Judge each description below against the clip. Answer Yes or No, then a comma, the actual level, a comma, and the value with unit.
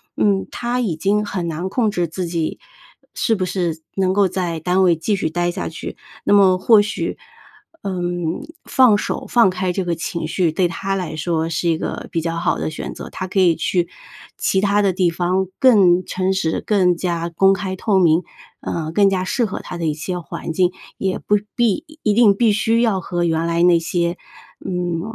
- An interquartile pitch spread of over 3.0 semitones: No, average, 2.7 semitones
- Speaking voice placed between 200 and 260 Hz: No, medium, 185 Hz